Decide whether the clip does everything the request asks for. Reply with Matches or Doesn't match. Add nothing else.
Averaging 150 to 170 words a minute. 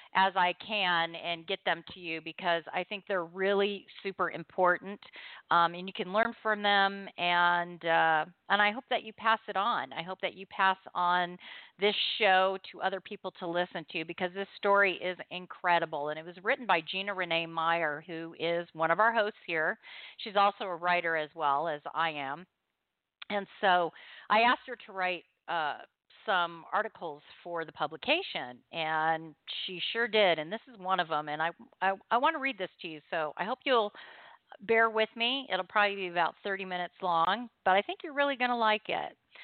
Doesn't match